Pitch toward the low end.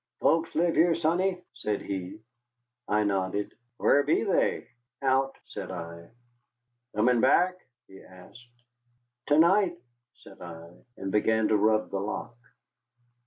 Yes: low, 115 Hz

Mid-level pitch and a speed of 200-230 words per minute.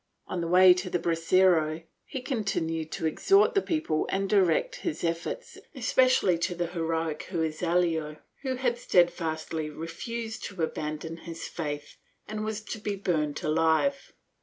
No: medium, 175 Hz; average, 145 wpm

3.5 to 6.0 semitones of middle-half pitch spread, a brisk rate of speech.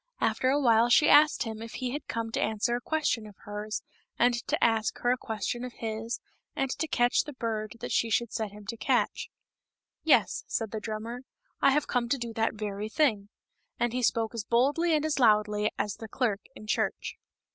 No: average, 2.7 semitones; fast, 215 wpm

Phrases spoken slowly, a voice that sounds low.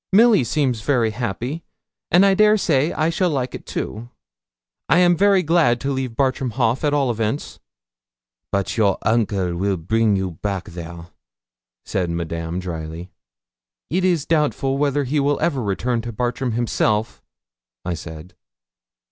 No: average, 150 wpm; low, 120 Hz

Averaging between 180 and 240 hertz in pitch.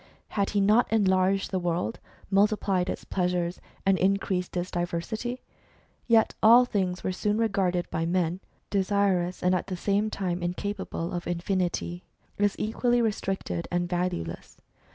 Yes: medium, 185 Hz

